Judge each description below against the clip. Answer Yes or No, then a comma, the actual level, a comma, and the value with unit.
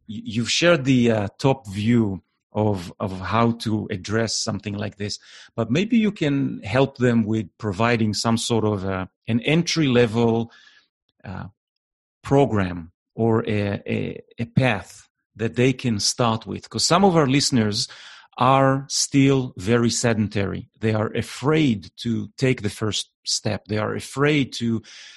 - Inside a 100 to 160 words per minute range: Yes, average, 150 wpm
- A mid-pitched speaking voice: No, low, 115 Hz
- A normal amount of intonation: Yes, average, 3.6 semitones